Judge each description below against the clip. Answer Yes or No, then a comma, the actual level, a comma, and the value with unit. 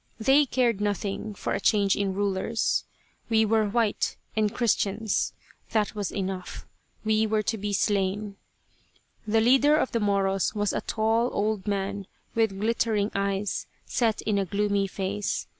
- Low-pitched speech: No, high, 210 Hz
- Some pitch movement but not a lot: No, narrow, 1.9 semitones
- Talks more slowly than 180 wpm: Yes, average, 150 wpm